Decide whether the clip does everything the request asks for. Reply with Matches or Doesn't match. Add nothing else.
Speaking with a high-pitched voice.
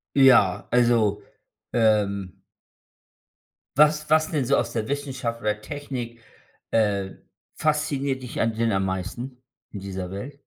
Doesn't match